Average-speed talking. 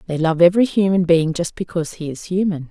No: fast, 220 wpm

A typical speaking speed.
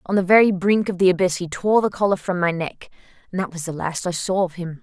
No: fast, 260 wpm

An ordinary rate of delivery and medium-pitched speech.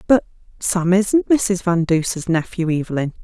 Yes: average, 150 wpm; medium, 180 Hz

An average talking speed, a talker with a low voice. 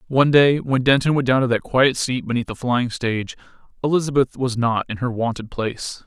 No: fast, 210 wpm; low, 125 Hz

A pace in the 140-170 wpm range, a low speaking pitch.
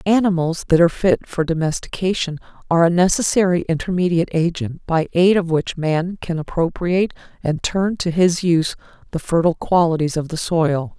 No: average, 160 wpm; medium, 170 Hz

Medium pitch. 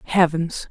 Yes: medium, 170 Hz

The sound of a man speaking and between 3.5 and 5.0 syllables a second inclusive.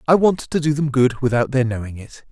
No: male; 5.6 syllables/s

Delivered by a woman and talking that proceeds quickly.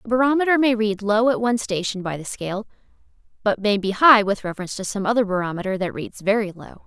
Yes: female; fast, 220 wpm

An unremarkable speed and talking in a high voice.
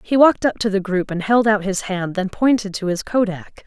No: fast, 260 wpm; high, 205 Hz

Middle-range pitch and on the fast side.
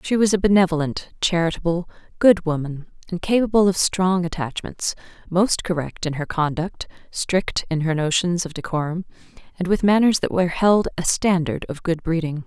No: medium, 175 Hz; average, 165 wpm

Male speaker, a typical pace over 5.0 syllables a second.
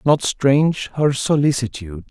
No: male; 4.8 syllables/s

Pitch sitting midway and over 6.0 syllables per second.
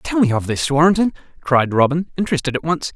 Yes: medium, 155 Hz; 6.3 syllables/s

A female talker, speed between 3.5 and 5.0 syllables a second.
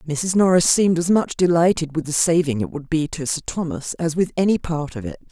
No: female; 5.7 syllables/s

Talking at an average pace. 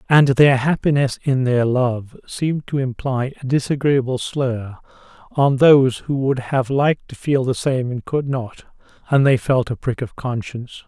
Yes: average, 170 wpm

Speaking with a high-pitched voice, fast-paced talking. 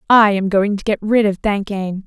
Yes: high, 205 Hz; fast, 230 wpm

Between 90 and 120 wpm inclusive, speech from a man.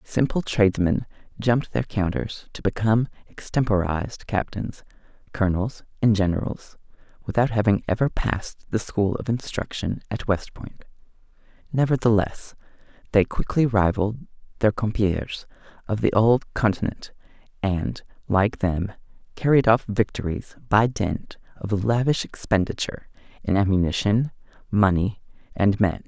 Yes: slow, 115 wpm; male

